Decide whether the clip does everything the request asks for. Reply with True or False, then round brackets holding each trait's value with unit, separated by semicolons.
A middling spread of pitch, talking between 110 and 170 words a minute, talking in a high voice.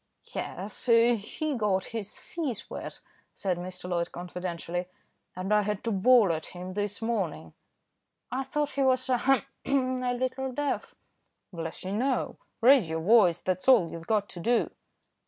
False (5.9 semitones; 155 wpm; 210 Hz)